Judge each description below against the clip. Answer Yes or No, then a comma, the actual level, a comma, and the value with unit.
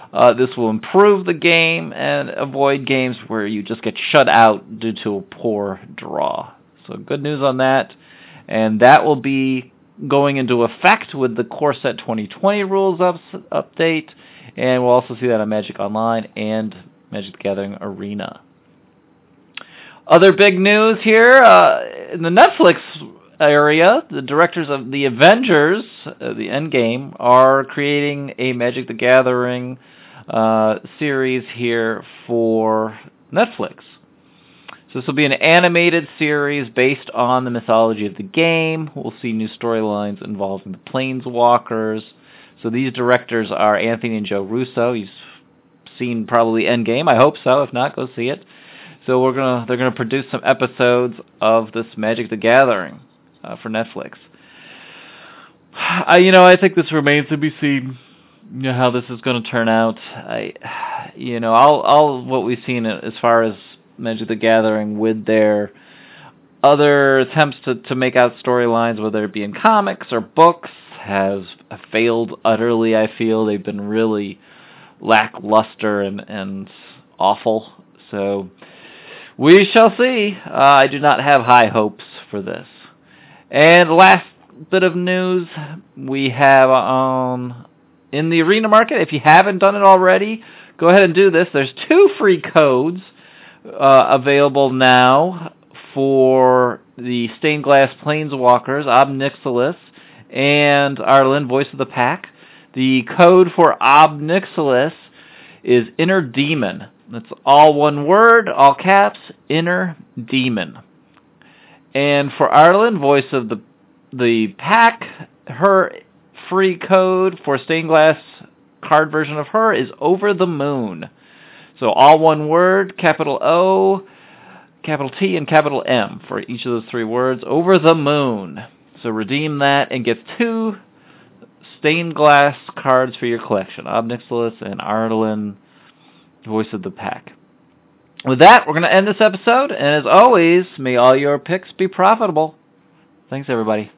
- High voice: No, low, 135 Hz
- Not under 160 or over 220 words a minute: No, average, 145 wpm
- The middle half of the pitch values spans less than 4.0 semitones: No, wide, 5.5 semitones